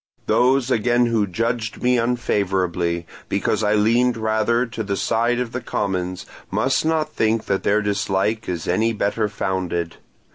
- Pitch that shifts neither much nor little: Yes, average, 3.4 semitones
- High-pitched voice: No, low, 110 Hz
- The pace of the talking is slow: No, average, 150 wpm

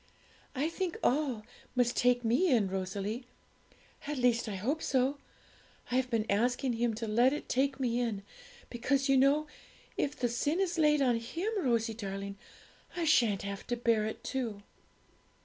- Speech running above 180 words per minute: No, average, 165 wpm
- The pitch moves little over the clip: No, average, 3.8 semitones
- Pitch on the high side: Yes, high, 245 Hz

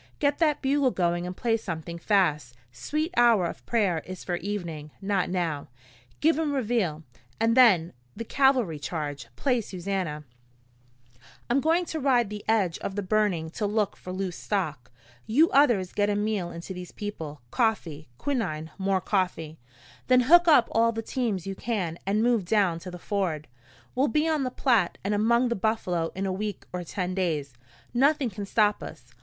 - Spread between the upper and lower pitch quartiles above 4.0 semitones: Yes, wide, 5.4 semitones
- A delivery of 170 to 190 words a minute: Yes, average, 175 wpm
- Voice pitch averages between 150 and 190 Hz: No, high, 200 Hz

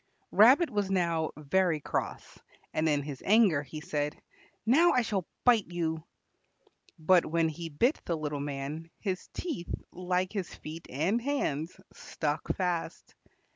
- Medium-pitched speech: Yes, medium, 170 Hz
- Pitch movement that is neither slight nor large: Yes, average, 4.6 semitones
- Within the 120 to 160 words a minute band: Yes, average, 140 wpm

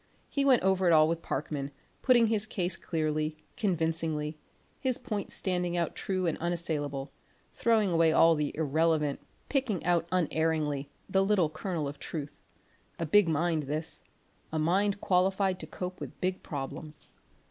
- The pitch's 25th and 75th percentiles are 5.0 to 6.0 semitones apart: No, average, 3.5 semitones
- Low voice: No, medium, 165 Hz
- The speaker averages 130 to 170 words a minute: Yes, average, 150 wpm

